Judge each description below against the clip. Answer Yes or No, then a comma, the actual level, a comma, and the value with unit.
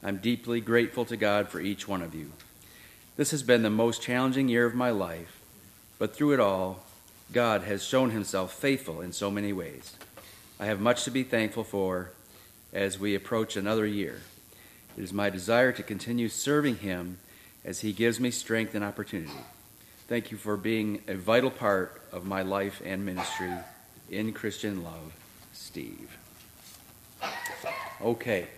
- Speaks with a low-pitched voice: Yes, low, 105 Hz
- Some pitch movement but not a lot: Yes, average, 3.1 semitones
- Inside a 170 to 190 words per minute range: No, average, 160 wpm